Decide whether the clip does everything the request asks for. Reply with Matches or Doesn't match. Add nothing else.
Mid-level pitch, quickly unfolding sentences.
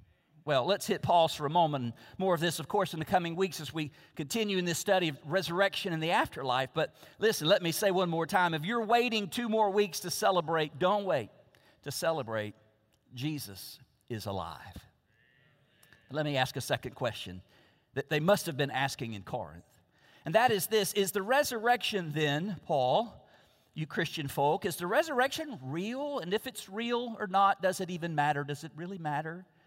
Doesn't match